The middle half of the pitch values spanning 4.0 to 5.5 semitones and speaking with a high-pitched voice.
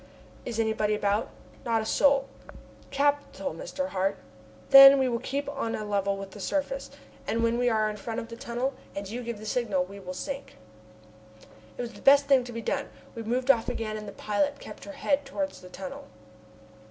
Yes: average, 4.5 semitones; high, 235 Hz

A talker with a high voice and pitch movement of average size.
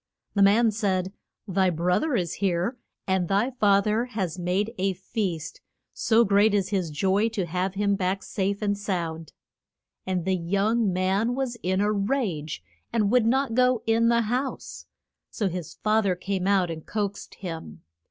Yes: high, 200 Hz; average, 3.2 semitones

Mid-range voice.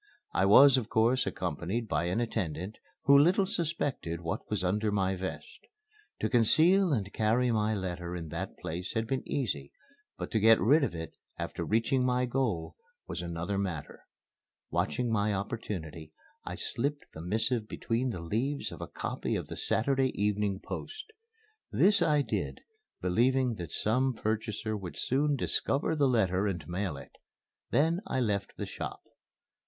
No: low, 110 Hz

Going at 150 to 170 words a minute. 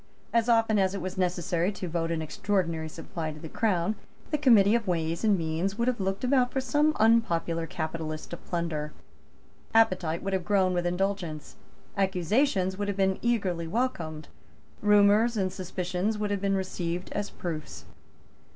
Yes: average, 165 wpm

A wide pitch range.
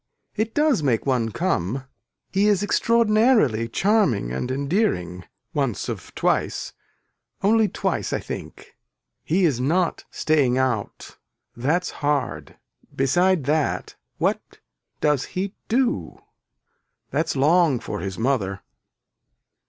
Yes: wide, 7.9 semitones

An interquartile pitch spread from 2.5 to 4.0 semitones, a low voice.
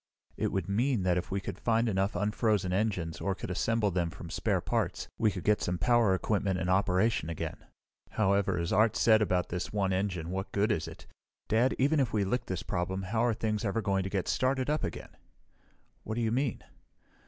Yes: average, 3.3 semitones; low, 100 Hz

